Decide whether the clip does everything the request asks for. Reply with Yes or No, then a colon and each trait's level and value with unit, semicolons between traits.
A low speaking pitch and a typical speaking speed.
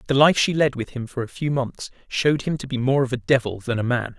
No: low, 130 Hz; fast, 300 wpm